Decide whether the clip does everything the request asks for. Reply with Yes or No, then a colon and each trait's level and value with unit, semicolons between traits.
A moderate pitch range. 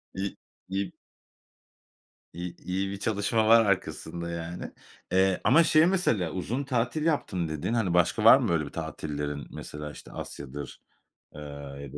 No: wide, 6.5 semitones